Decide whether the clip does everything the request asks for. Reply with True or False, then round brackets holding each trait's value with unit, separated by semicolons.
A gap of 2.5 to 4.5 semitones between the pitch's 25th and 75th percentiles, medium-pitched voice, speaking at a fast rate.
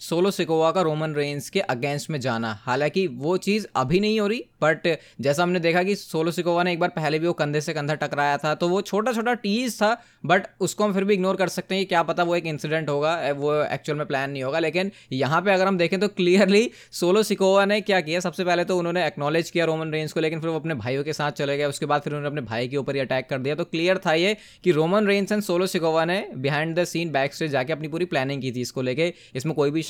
True (4.1 semitones; 165 Hz; 265 wpm)